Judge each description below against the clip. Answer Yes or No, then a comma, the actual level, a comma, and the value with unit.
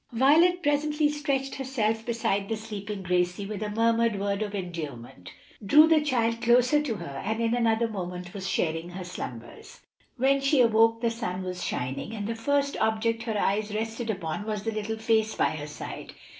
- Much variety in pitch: No, average, 3.6 semitones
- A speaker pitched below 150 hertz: No, high, 220 Hz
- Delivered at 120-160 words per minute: No, average, 185 wpm